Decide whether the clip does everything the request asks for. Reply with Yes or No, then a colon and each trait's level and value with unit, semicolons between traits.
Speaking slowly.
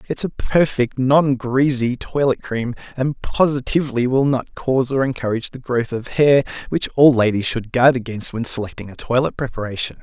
No: average, 180 wpm